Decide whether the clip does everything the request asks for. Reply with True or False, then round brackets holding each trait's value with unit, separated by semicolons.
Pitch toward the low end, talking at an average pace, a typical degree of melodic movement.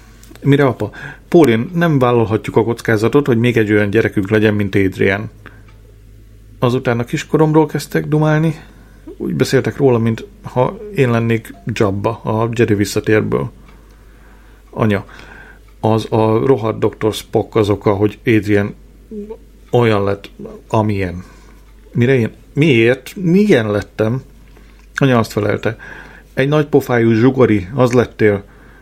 True (115 Hz; 120 wpm; 3.7 semitones)